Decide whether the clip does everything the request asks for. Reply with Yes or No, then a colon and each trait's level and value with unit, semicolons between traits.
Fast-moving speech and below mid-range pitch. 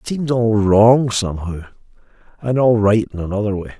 No: average, 160 wpm; low, 110 Hz